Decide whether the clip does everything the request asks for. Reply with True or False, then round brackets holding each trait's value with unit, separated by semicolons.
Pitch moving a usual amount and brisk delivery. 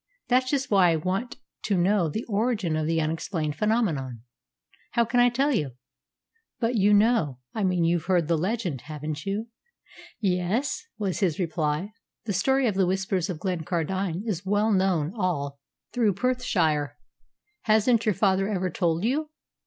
False (5.0 semitones; 160 wpm)